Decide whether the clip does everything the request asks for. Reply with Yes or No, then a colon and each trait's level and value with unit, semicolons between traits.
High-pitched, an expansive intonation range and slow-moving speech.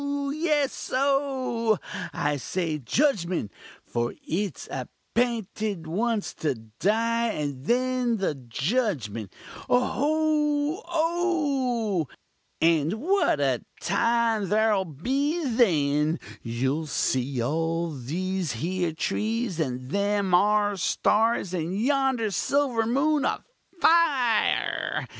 Yes: high, 210 Hz; wide, 8.5 semitones; slow, 95 wpm